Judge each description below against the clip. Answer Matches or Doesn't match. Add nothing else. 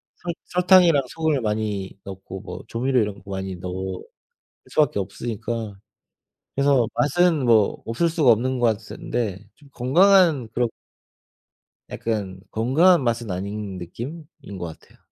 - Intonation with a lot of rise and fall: Matches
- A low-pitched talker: Matches